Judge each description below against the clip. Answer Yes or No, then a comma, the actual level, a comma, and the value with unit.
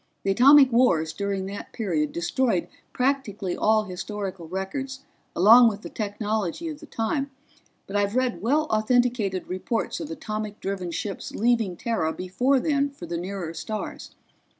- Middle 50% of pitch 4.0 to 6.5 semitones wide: Yes, average, 4.8 semitones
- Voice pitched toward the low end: No, high, 210 Hz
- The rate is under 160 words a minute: Yes, average, 150 wpm